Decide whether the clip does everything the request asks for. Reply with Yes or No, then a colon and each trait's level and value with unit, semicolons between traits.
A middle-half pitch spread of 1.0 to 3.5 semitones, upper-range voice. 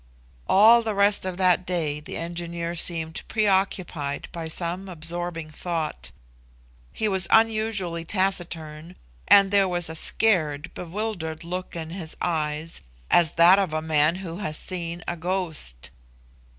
No: average, 2.9 semitones; medium, 175 Hz